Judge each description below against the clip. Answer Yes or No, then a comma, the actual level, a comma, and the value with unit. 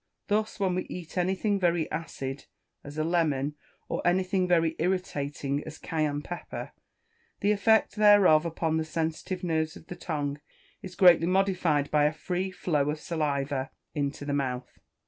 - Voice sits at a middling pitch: Yes, medium, 165 Hz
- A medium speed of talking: Yes, average, 155 wpm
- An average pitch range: Yes, average, 3.8 semitones